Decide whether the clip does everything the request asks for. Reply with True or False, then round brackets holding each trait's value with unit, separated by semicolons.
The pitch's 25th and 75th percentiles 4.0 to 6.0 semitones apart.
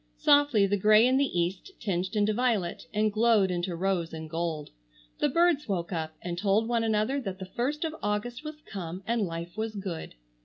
True (5.2 semitones)